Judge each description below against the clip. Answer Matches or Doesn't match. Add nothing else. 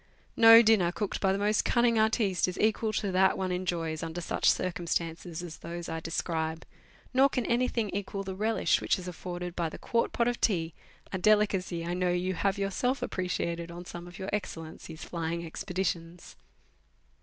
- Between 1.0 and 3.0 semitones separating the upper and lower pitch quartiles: Doesn't match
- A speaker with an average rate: Matches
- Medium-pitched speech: Matches